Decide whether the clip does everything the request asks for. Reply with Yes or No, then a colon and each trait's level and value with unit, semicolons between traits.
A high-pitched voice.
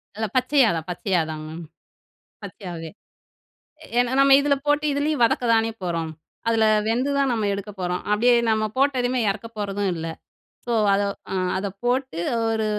Yes: high, 220 Hz